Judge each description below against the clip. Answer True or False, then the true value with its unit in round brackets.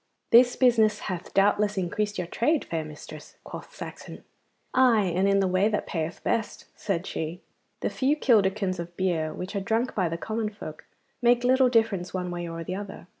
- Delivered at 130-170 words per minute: False (185 wpm)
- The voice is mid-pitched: False (195 Hz)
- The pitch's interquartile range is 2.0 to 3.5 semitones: False (4.3 semitones)